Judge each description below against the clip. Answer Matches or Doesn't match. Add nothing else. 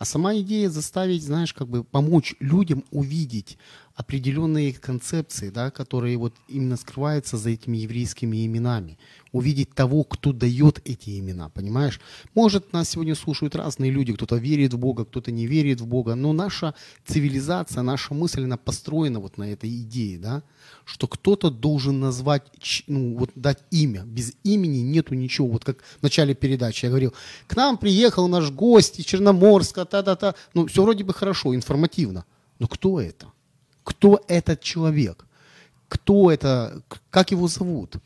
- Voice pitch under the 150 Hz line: Matches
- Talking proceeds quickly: Matches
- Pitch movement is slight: Doesn't match